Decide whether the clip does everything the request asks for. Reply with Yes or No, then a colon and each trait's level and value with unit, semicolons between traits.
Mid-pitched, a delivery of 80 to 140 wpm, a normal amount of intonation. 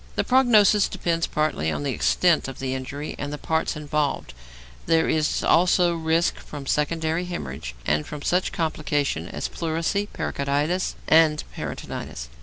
No: medium, 155 Hz; average, 150 wpm; average, 3.3 semitones